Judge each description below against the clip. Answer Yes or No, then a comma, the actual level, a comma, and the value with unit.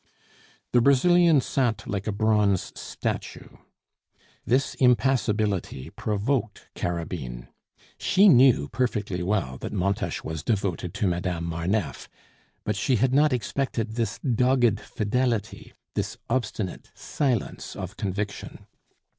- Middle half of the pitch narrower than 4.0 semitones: No, average, 4.8 semitones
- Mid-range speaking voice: No, low, 110 Hz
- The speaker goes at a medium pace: No, slow, 110 wpm